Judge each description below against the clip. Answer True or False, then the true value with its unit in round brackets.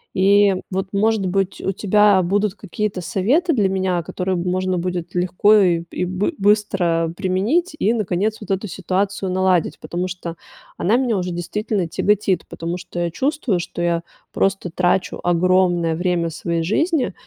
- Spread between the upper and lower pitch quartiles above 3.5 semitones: False (2.7 semitones)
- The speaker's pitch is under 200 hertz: True (185 Hz)